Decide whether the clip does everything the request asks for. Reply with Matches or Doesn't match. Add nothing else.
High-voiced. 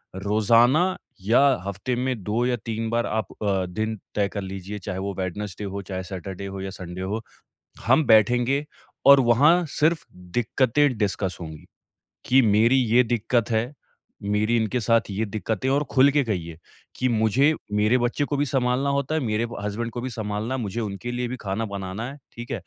Doesn't match